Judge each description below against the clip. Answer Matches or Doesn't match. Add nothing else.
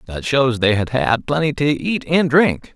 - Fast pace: Matches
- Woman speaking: Doesn't match